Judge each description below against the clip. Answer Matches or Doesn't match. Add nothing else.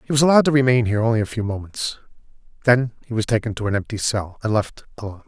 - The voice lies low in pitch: Matches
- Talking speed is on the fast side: Matches